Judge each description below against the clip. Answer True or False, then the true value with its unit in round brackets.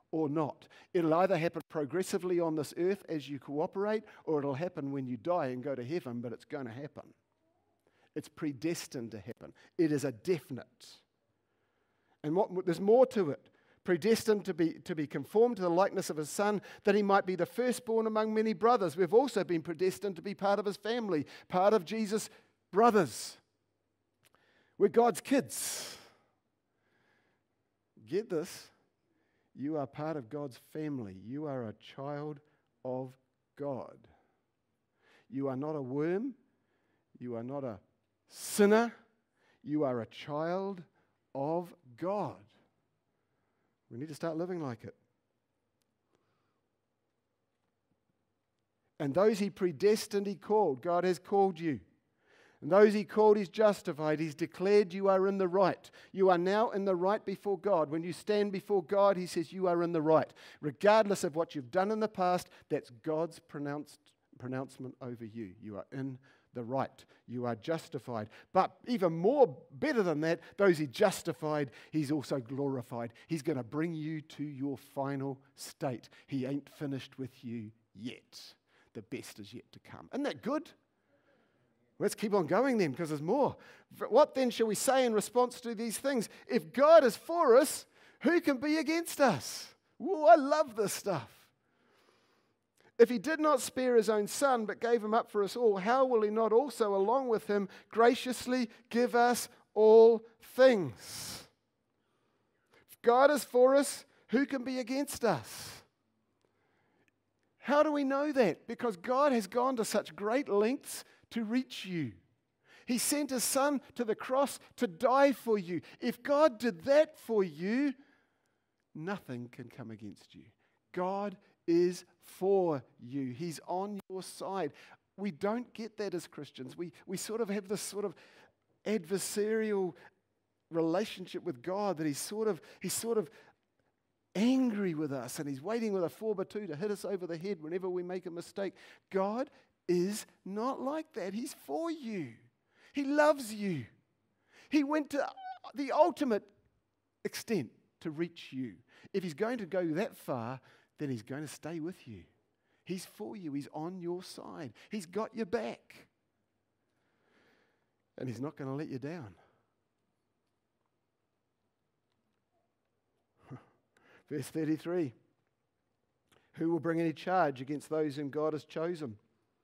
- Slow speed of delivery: False (160 wpm)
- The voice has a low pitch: False (185 Hz)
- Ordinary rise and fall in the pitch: False (7.0 semitones)